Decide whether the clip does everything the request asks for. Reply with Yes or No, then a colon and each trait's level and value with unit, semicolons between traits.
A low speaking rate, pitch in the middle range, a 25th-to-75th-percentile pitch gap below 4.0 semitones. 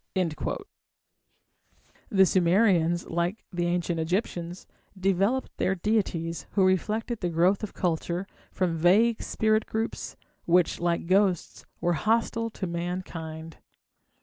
Yes: slow, 110 wpm; medium, 180 Hz; average, 3.3 semitones